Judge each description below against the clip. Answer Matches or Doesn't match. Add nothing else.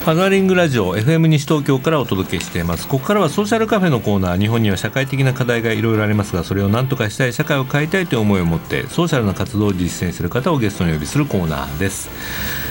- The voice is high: Doesn't match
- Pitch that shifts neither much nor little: Doesn't match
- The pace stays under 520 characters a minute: Doesn't match